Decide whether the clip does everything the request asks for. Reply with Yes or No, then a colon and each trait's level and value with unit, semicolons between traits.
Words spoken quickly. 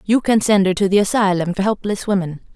Yes: fast, 235 wpm